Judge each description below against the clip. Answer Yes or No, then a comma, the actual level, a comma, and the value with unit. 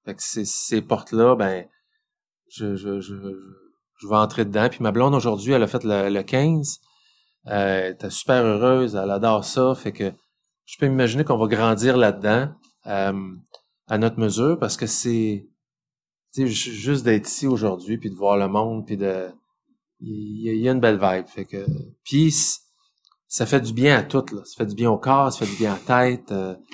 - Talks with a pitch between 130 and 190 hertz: No, low, 115 Hz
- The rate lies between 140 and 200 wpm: No, average, 210 wpm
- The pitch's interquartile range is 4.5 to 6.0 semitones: Yes, average, 4.9 semitones